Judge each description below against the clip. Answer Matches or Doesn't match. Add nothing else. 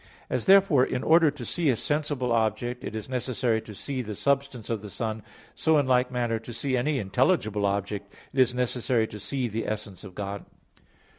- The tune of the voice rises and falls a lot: Doesn't match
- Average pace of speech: Doesn't match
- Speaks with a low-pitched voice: Matches